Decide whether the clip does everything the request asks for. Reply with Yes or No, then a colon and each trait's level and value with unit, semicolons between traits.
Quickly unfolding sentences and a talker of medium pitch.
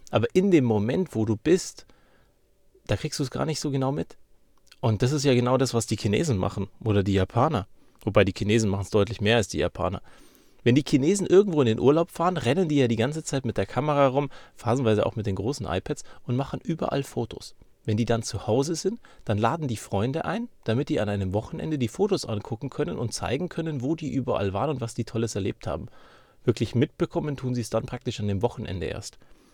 No: fast, 225 wpm; low, 120 Hz